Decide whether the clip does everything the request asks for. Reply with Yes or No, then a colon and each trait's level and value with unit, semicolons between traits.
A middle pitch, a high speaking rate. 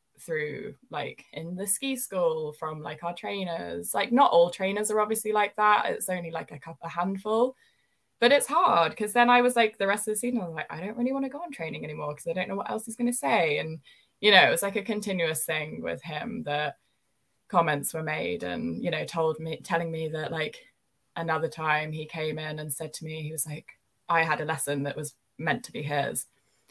Yes: medium, 165 Hz; fast, 240 wpm